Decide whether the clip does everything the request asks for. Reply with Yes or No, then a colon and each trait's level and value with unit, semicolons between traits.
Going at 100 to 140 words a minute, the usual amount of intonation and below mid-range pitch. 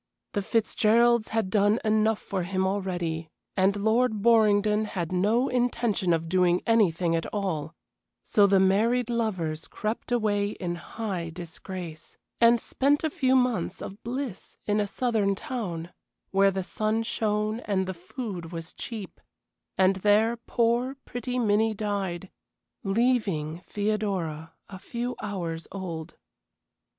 No: slow, 135 wpm; average, 3.8 semitones; high, 205 Hz